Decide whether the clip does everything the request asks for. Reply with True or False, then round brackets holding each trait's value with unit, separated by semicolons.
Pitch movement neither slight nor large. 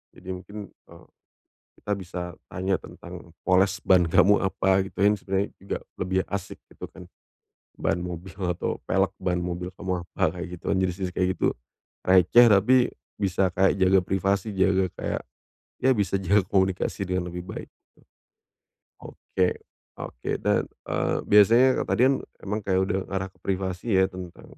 False (1.4 semitones)